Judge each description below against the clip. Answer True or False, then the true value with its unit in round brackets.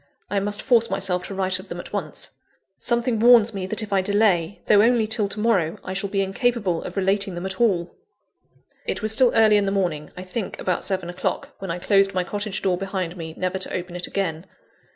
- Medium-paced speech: False (225 wpm)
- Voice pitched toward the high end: True (195 Hz)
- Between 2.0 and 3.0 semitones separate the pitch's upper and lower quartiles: True (2.6 semitones)